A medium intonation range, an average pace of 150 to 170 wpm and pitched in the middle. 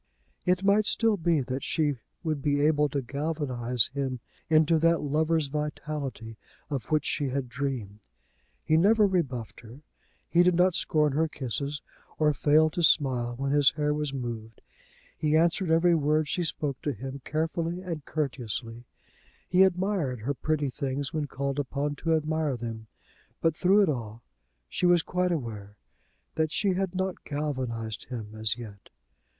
Yes: average, 4.1 semitones; average, 160 wpm; medium, 150 Hz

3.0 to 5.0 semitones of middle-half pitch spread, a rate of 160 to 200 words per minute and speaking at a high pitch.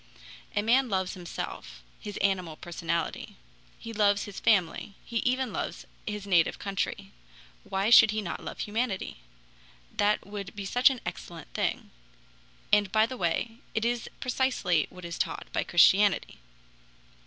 No: average, 3.7 semitones; average, 145 wpm; high, 205 Hz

